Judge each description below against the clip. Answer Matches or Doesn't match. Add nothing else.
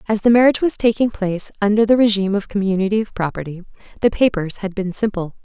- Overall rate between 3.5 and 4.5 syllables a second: Doesn't match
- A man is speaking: Doesn't match